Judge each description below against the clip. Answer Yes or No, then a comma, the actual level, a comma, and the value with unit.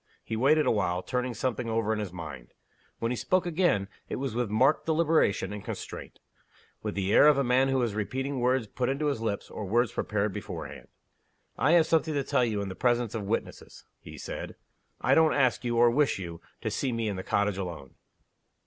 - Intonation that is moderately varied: Yes, average, 4.7 semitones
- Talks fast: Yes, fast, 210 wpm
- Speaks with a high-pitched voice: No, low, 120 Hz